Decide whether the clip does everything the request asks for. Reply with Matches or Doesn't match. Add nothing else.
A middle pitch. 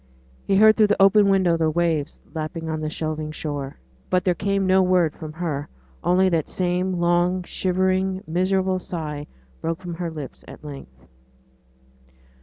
Matches